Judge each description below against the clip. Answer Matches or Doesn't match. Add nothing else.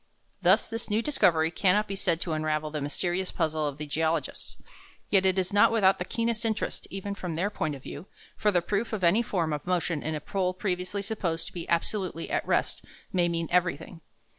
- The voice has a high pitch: Doesn't match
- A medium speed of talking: Doesn't match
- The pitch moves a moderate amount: Matches